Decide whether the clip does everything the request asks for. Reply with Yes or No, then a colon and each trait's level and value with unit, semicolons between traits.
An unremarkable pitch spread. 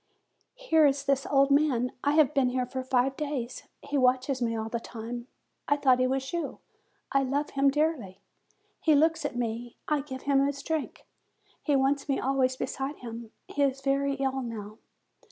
No: narrow, 2.2 semitones